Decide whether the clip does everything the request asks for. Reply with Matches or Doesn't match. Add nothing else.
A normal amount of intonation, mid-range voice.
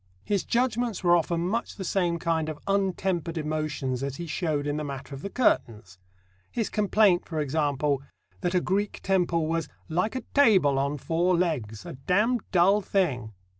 Matches